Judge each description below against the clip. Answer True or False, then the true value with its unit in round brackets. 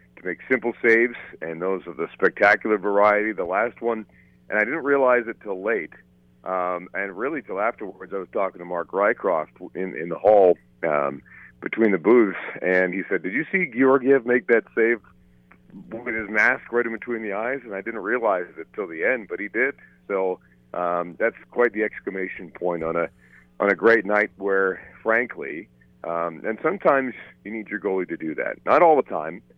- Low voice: True (95 Hz)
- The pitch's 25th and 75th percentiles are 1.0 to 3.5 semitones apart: False (5.1 semitones)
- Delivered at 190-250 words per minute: True (195 wpm)